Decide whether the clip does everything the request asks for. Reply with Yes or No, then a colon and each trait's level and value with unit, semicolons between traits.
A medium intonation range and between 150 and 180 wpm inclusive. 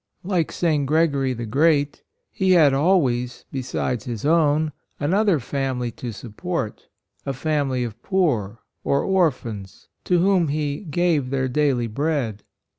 No: average, 4.9 semitones; average, 140 wpm